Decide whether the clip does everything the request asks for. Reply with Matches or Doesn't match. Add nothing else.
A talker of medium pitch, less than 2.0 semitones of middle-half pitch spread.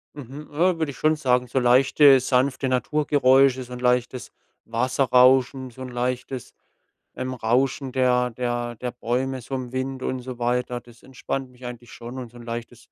Doesn't match